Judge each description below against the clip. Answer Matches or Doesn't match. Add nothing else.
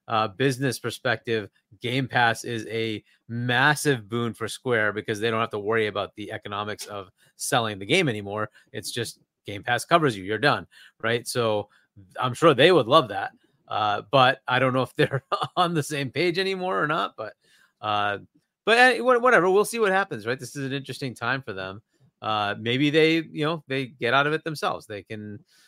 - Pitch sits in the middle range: Doesn't match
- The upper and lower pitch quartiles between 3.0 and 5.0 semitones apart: Doesn't match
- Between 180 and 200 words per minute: Matches